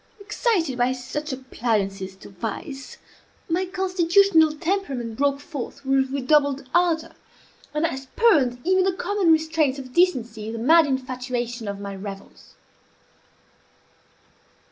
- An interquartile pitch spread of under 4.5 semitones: No, wide, 5.4 semitones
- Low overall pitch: No, very high, 275 Hz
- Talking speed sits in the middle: No, slow, 120 wpm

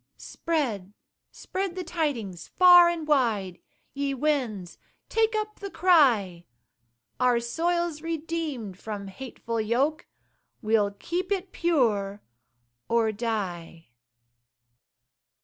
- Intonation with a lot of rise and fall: Yes, wide, 8.3 semitones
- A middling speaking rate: No, slow, 95 wpm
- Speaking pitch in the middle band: No, very high, 260 Hz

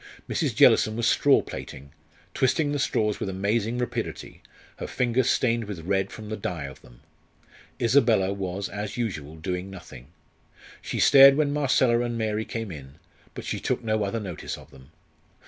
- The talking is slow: No, average, 165 wpm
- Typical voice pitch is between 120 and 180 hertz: No, low, 110 Hz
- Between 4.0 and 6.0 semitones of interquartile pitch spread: Yes, average, 4.4 semitones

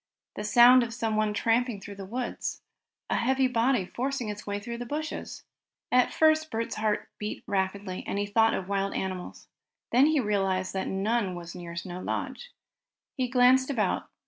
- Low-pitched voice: No, high, 220 Hz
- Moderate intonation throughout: Yes, average, 4.2 semitones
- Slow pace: No, average, 170 wpm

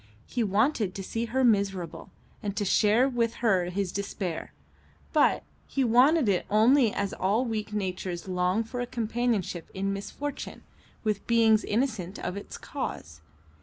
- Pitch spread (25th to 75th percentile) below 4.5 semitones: Yes, average, 3.7 semitones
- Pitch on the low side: No, high, 210 Hz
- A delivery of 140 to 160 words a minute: Yes, average, 150 wpm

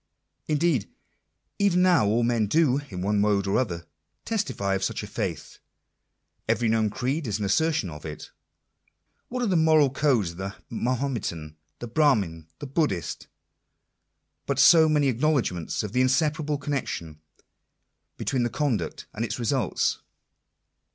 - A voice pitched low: Yes, low, 125 Hz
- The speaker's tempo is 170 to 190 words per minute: No, average, 140 wpm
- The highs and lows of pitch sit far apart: Yes, wide, 6.9 semitones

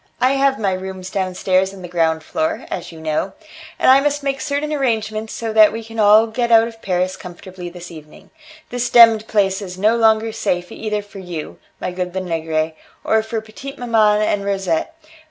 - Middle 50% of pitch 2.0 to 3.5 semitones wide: No, average, 3.9 semitones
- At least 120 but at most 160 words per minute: No, average, 190 wpm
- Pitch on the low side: No, high, 210 Hz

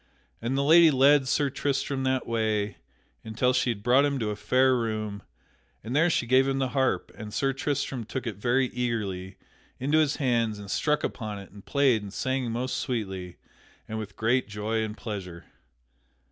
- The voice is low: Yes, low, 120 Hz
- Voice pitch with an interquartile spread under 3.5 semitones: No, average, 3.9 semitones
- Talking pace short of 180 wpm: No, average, 185 wpm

